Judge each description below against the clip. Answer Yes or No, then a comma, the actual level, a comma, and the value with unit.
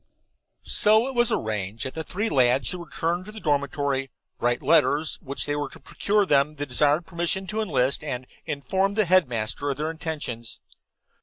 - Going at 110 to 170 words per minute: No, average, 180 wpm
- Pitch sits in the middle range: Yes, medium, 150 Hz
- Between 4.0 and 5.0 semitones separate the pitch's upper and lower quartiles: No, wide, 5.5 semitones